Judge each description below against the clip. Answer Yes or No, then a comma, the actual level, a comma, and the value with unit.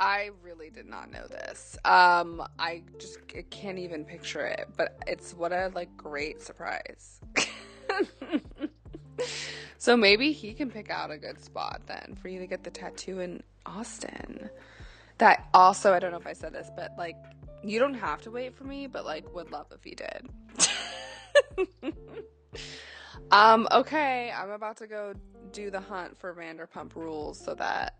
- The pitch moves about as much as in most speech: No, wide, 6.3 semitones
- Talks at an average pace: Yes, average, 165 wpm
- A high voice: Yes, high, 200 Hz